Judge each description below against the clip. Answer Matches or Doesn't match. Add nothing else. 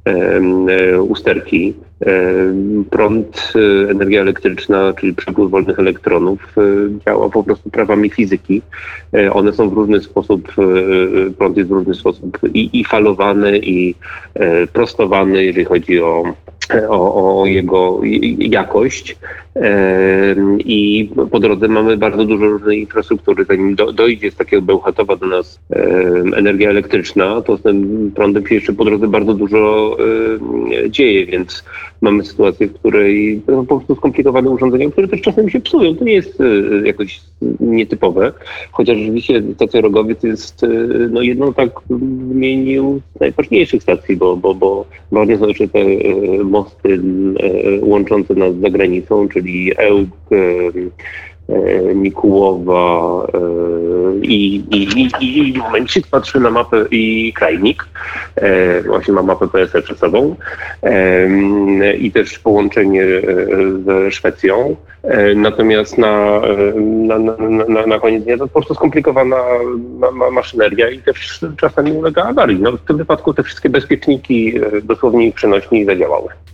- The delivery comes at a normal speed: Matches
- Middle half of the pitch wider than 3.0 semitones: Matches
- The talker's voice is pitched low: Matches